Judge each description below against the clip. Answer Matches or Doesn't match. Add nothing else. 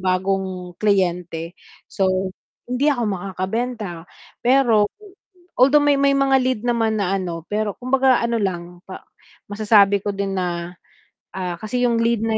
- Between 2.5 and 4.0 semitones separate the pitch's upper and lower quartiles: Doesn't match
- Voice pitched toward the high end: Matches